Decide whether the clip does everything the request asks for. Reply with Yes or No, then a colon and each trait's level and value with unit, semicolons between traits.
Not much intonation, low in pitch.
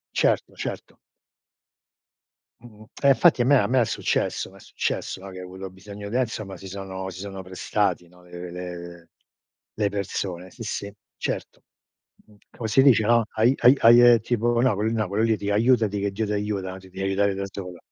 No: average, 3.3 semitones; low, 100 Hz